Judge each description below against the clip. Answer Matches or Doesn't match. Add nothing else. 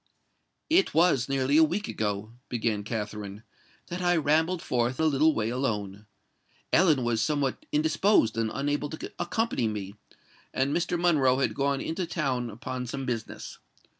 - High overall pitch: Doesn't match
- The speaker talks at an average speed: Matches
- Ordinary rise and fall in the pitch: Doesn't match